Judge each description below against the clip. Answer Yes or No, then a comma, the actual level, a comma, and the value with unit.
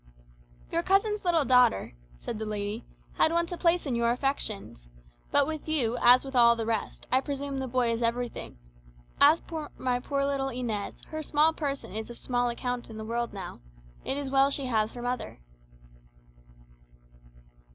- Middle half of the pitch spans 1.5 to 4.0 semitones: Yes, average, 3.6 semitones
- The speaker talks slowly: No, average, 175 wpm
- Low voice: No, very high, 255 Hz